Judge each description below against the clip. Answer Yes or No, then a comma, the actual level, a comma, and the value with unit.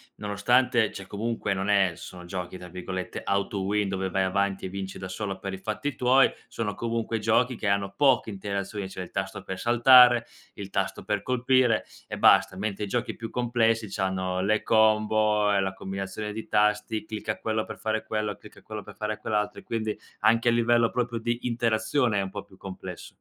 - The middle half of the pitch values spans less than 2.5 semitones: No, average, 2.9 semitones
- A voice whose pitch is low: Yes, low, 105 Hz